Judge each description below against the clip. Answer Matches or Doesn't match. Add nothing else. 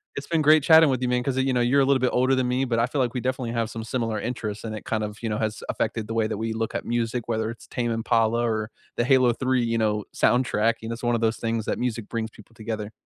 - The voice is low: Matches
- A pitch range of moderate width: Doesn't match